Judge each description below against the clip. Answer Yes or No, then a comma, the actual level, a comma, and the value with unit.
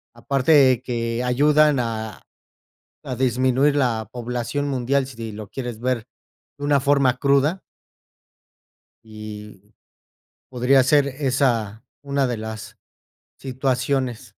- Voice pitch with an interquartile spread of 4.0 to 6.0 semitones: No, average, 3.1 semitones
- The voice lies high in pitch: No, low, 130 Hz